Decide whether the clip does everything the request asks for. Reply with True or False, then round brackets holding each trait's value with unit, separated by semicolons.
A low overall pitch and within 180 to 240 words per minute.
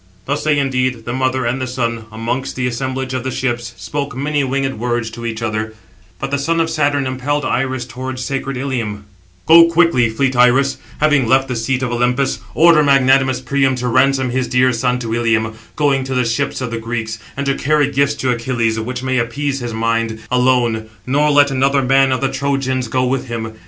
True (130 Hz; 205 wpm)